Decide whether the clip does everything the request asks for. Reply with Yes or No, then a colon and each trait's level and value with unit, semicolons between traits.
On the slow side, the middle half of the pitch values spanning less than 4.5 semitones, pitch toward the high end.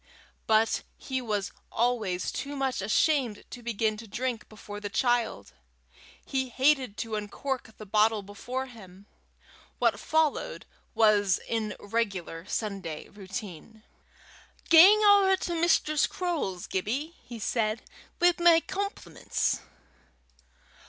No: slow, 115 wpm; average, 5.0 semitones; high, 225 Hz